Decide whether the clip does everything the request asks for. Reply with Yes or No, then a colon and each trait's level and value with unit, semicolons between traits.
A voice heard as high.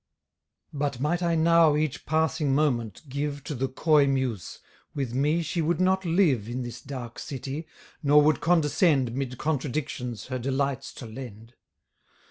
No: medium, 140 Hz